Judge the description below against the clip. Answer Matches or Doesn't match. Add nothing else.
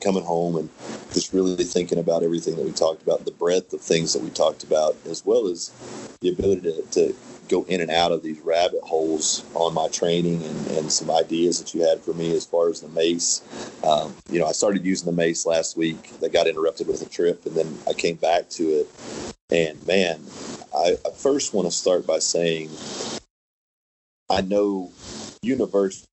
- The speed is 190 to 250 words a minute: Matches